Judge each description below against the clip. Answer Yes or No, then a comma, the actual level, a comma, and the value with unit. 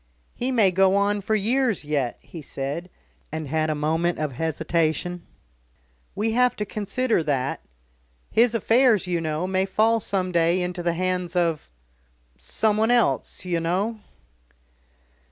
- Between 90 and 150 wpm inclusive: Yes, average, 140 wpm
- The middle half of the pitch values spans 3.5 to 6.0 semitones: Yes, average, 4.8 semitones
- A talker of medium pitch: Yes, medium, 180 Hz